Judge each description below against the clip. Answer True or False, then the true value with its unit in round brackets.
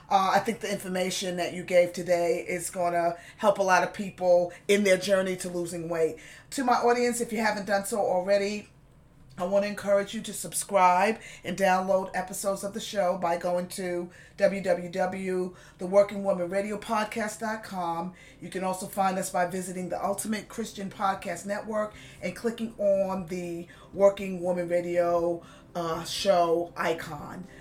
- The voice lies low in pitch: False (185 Hz)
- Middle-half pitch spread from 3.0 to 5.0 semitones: False (2.4 semitones)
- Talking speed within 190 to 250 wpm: False (155 wpm)